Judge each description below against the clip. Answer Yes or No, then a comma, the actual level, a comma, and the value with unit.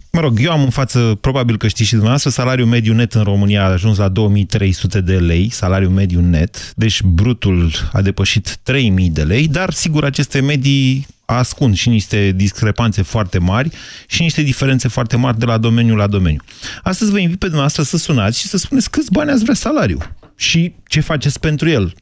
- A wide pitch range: Yes, wide, 6.1 semitones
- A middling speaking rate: No, fast, 195 wpm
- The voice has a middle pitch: No, low, 115 Hz